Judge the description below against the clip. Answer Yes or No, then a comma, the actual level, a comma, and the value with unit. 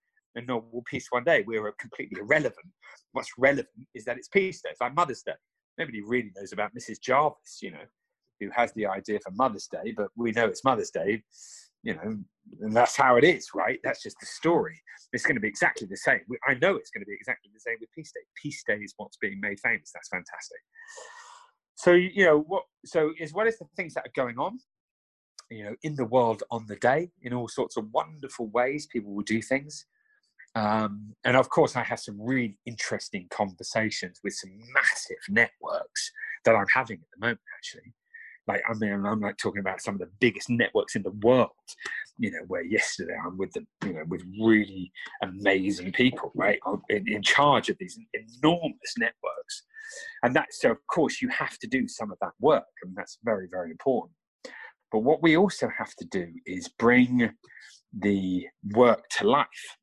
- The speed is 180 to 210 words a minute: Yes, average, 200 wpm